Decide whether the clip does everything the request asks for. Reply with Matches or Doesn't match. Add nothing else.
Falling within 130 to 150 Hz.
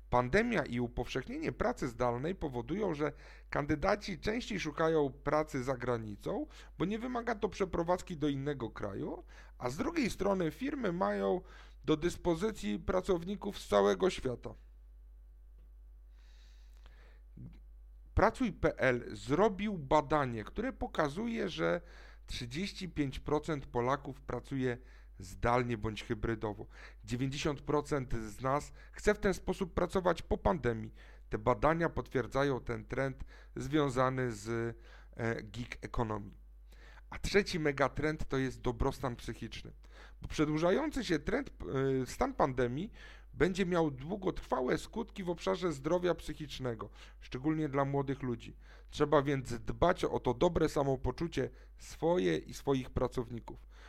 Matches